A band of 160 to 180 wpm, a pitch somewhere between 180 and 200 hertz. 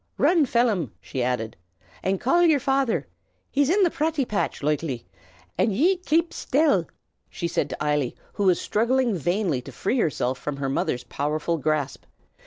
Yes: average, 165 wpm; high, 190 Hz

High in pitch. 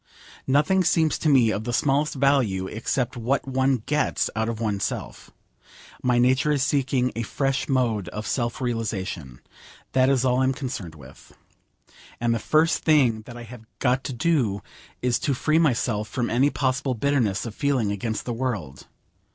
No: low, 125 Hz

